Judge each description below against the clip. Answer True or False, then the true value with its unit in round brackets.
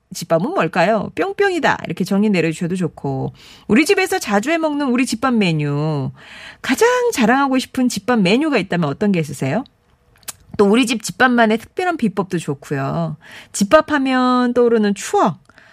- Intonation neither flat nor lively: False (7.4 semitones)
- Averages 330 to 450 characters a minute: True (335 characters per minute)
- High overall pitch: True (215 Hz)